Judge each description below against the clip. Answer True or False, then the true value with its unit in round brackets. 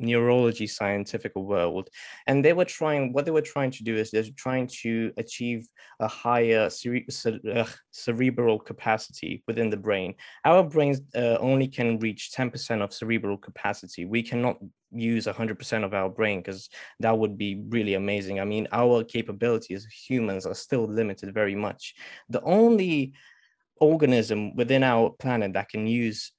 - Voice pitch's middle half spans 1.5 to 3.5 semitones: True (2.7 semitones)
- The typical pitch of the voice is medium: False (115 Hz)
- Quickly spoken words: False (160 wpm)